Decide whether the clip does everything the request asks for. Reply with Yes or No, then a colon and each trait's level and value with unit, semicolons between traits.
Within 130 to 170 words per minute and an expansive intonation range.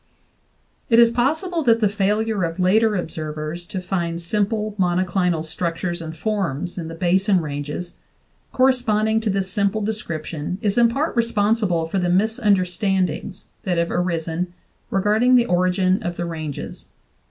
No: average, 145 wpm; average, 4.0 semitones